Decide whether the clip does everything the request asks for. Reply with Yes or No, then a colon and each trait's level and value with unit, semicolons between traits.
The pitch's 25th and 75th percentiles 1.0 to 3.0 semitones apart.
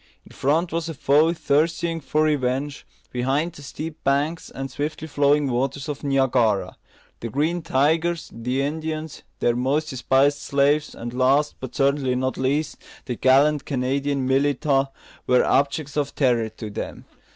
Yes: narrow, 2.6 semitones